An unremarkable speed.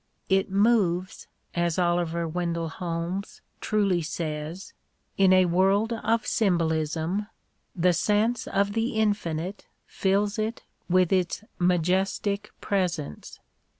No: slow, 115 wpm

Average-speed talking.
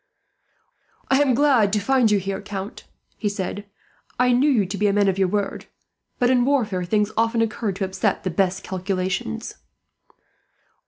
Yes: average, 170 wpm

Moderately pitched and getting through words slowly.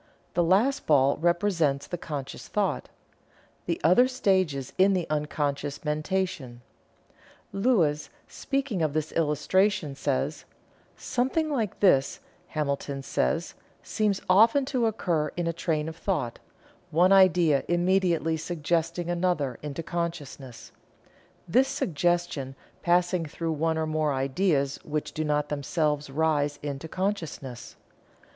Yes: medium, 160 Hz; slow, 120 wpm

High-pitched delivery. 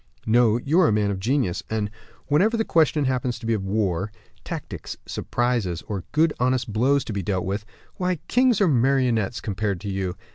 No: low, 115 Hz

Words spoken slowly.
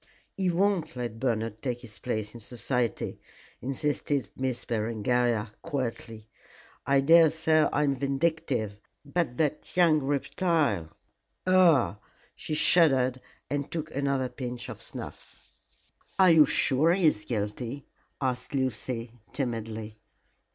Yes: slow, 115 wpm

